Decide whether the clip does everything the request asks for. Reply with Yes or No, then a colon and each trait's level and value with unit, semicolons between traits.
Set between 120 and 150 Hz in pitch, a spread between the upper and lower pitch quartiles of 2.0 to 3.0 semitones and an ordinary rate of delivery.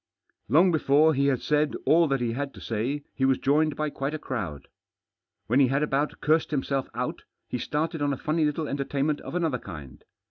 No: medium, 140 Hz; narrow, 2.5 semitones; fast, 210 wpm